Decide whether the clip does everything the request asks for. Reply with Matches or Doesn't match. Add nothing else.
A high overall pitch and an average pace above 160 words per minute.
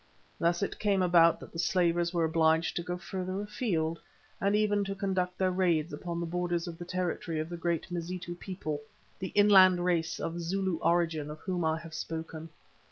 Doesn't match